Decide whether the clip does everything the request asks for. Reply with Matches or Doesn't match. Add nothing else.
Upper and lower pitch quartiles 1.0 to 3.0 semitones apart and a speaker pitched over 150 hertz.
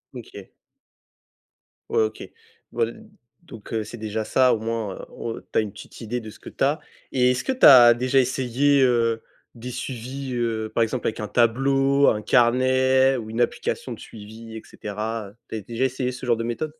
Doesn't match